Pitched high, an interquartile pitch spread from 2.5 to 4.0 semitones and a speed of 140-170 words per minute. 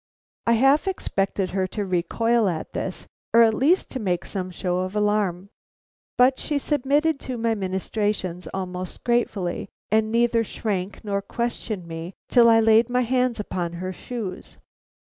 No: high, 215 Hz; average, 4.4 semitones; average, 155 wpm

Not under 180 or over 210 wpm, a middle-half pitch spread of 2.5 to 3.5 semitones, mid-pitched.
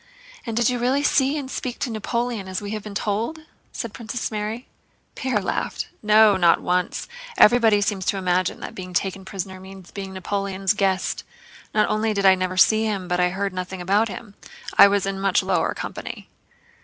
No: average, 185 wpm; average, 2.8 semitones; high, 200 Hz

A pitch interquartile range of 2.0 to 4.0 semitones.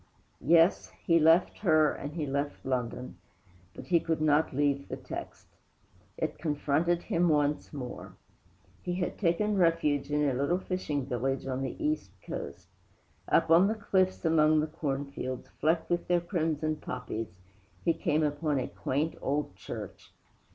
Yes: average, 3.3 semitones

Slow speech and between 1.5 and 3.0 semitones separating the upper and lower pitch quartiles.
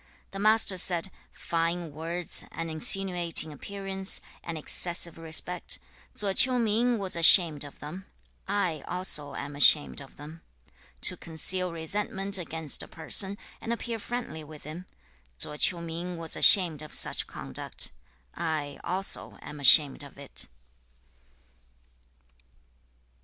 No: slow, 125 wpm; average, 3.7 semitones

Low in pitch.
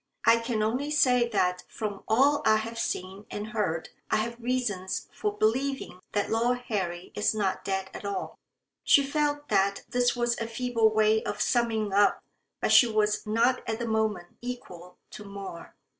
No: high, 220 Hz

